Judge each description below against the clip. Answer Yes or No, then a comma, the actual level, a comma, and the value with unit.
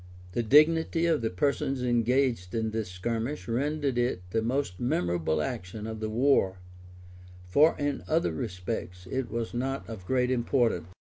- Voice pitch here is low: Yes, low, 120 Hz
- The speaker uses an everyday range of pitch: No, wide, 6.1 semitones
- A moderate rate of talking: Yes, average, 150 wpm